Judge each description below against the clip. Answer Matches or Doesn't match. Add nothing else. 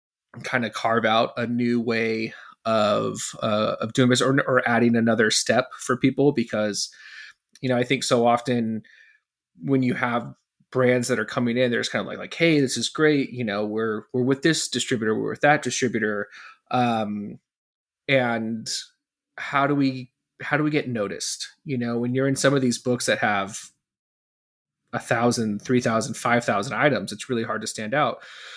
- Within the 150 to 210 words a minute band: Matches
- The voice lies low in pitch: Matches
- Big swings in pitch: Doesn't match